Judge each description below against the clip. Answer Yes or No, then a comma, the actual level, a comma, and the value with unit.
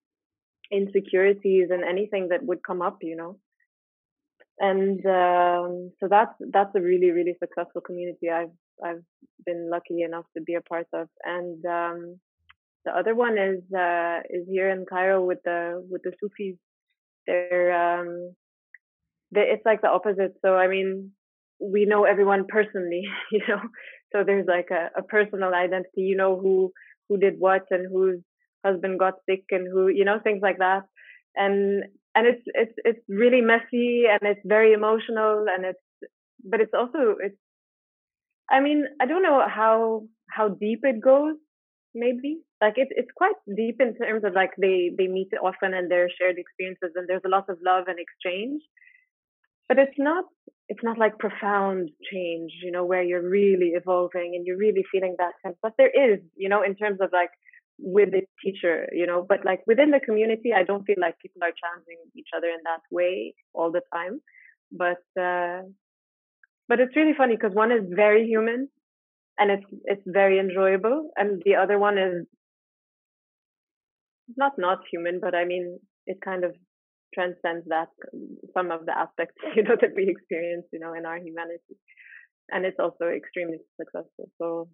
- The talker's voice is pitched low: No, high, 190 Hz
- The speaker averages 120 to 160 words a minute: No, average, 175 wpm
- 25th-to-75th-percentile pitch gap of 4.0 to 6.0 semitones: No, average, 3.5 semitones